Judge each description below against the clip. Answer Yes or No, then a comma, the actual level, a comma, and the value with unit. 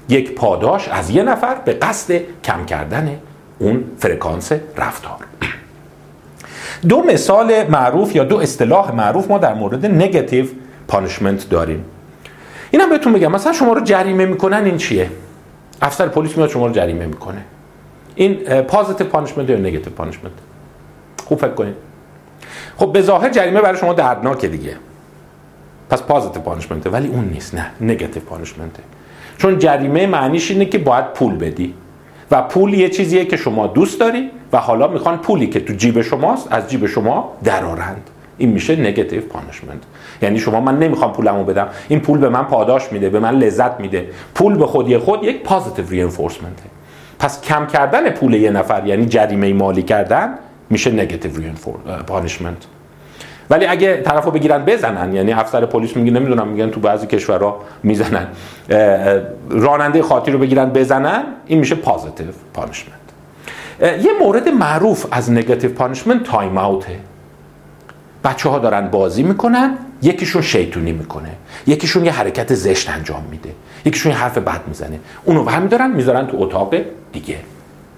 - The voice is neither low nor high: No, low, 125 Hz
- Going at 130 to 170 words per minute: Yes, average, 150 wpm